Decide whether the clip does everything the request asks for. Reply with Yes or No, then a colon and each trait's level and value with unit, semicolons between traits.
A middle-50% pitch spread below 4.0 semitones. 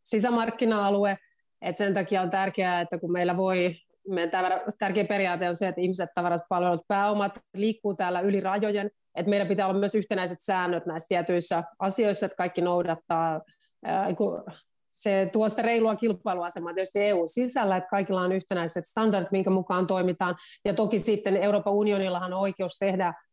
Yes: narrow, 2.4 semitones